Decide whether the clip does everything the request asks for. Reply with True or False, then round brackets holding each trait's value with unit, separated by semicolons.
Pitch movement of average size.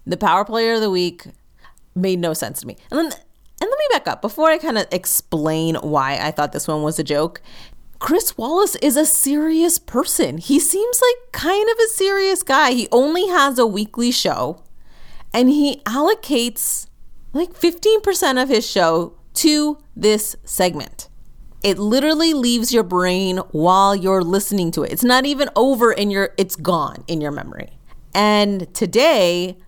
False (8.6 semitones)